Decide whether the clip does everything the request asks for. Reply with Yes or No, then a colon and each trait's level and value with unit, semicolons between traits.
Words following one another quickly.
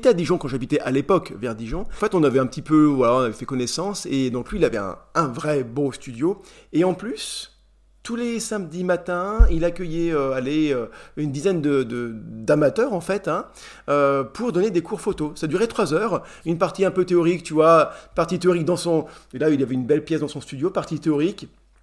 Yes: fast, 230 wpm